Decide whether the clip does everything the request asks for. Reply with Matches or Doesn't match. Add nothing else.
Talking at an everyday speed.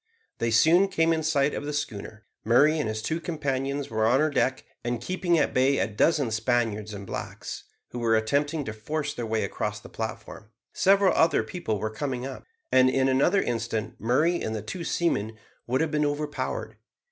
Matches